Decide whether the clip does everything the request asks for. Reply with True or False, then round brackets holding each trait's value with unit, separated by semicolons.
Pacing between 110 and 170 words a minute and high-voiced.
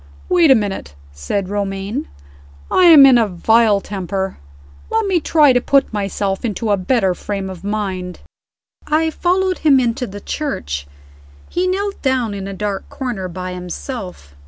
True (160 wpm; 210 Hz)